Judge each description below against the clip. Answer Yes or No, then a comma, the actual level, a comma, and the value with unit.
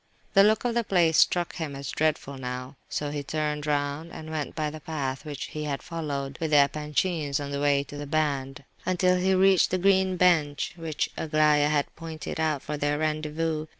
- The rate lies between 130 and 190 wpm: No, average, 200 wpm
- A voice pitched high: No, medium, 155 Hz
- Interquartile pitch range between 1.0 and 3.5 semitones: Yes, narrow, 2.4 semitones